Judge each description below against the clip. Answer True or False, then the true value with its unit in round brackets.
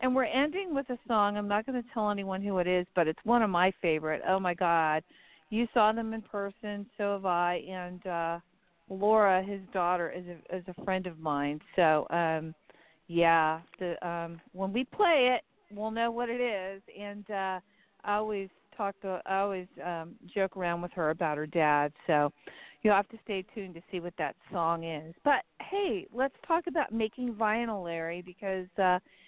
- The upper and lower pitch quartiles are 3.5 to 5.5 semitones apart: True (3.9 semitones)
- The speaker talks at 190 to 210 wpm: True (195 wpm)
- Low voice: False (190 Hz)